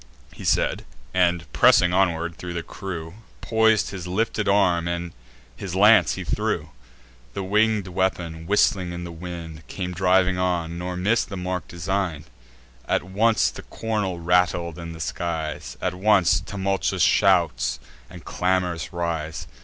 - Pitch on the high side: No, very low, 90 Hz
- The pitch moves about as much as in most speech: No, narrow, 2.2 semitones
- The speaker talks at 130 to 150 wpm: Yes, average, 145 wpm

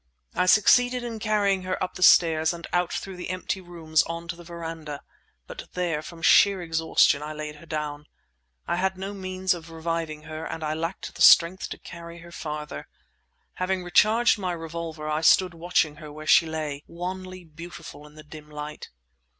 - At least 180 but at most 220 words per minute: Yes, average, 185 wpm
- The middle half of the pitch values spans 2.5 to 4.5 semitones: Yes, average, 3.0 semitones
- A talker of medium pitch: Yes, medium, 170 Hz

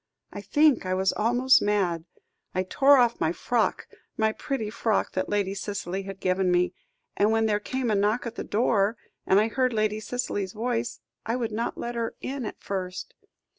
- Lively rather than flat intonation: No, average, 3.6 semitones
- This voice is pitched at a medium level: No, high, 215 Hz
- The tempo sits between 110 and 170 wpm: No, average, 190 wpm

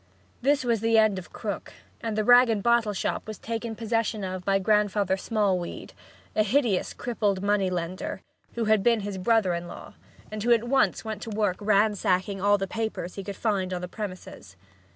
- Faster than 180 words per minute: Yes, average, 195 wpm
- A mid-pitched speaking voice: No, high, 210 Hz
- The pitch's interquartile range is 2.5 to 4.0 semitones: Yes, average, 2.9 semitones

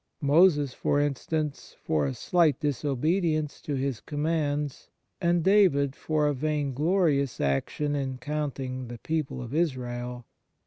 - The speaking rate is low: Yes, slow, 125 wpm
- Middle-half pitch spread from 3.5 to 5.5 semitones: No, average, 3.0 semitones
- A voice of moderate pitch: Yes, medium, 145 Hz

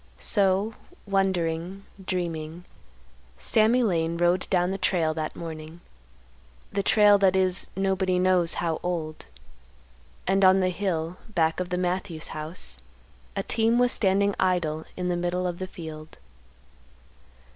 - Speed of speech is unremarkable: No, slow, 130 wpm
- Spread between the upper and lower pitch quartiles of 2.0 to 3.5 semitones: Yes, average, 2.9 semitones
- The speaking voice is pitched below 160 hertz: No, medium, 180 Hz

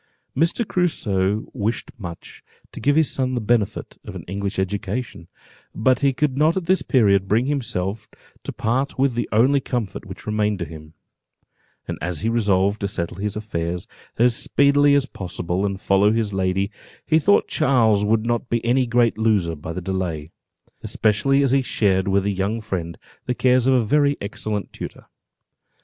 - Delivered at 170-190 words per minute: Yes, average, 175 wpm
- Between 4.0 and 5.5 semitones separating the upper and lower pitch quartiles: Yes, average, 4.9 semitones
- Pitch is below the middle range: Yes, low, 110 Hz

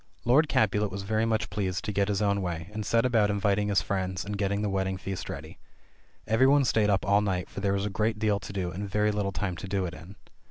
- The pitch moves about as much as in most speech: No, narrow, 1.7 semitones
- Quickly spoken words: Yes, fast, 255 wpm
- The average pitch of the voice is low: Yes, low, 100 Hz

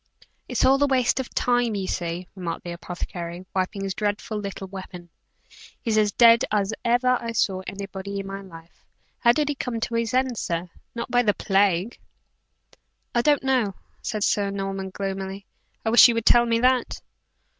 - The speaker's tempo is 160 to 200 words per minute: Yes, average, 180 wpm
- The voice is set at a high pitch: Yes, high, 205 Hz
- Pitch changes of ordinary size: Yes, average, 3.7 semitones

